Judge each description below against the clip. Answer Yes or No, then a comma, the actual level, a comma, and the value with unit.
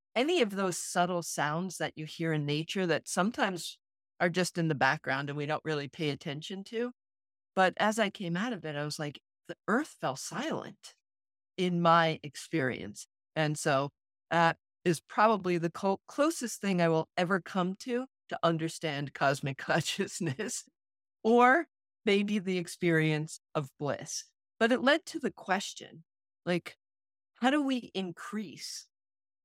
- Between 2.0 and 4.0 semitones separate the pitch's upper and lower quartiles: No, average, 4.9 semitones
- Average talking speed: Yes, average, 155 wpm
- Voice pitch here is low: No, medium, 175 Hz